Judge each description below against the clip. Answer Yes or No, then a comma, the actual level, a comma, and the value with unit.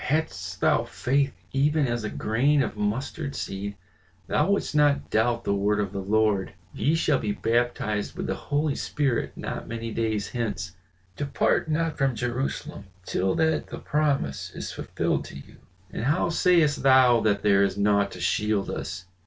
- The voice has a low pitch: Yes, low, 115 Hz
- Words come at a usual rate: Yes, average, 170 wpm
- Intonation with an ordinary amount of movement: No, wide, 5.9 semitones